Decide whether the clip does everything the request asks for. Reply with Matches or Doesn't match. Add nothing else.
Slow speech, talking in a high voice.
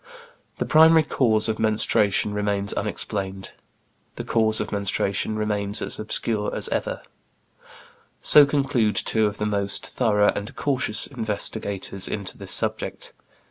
Doesn't match